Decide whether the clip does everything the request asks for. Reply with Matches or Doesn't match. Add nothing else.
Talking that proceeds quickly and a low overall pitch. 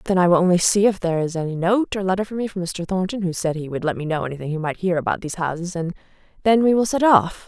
Doesn't match